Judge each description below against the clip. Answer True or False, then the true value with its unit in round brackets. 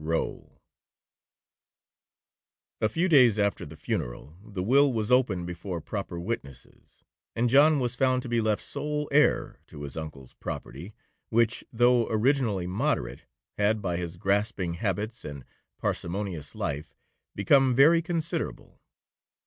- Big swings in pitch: True (6.5 semitones)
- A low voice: True (105 Hz)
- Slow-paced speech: True (130 wpm)